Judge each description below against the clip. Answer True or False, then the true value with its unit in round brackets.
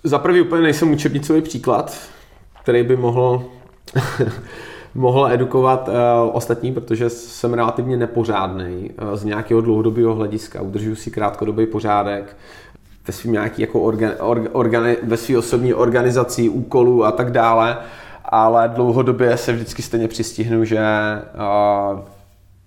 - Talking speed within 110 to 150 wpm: True (120 wpm)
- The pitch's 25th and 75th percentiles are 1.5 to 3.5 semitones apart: True (2.5 semitones)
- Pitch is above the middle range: False (115 Hz)